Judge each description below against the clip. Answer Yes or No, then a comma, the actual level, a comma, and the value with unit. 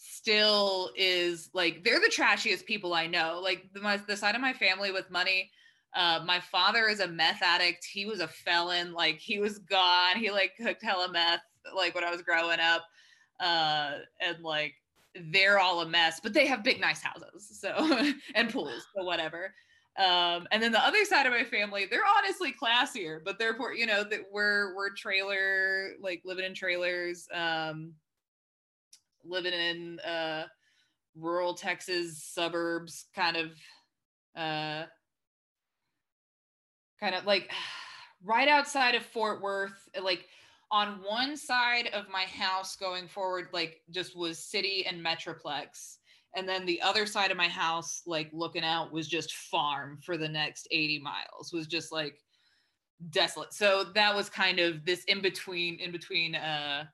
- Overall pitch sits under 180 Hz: No, medium, 185 Hz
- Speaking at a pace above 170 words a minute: No, average, 165 wpm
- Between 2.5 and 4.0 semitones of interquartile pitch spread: Yes, average, 3.5 semitones